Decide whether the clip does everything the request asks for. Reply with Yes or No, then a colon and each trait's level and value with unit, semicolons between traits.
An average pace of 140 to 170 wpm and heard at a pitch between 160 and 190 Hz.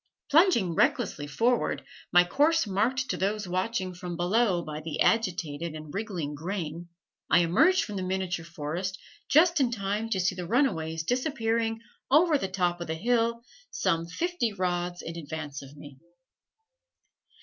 Yes: average, 150 wpm; medium, 185 Hz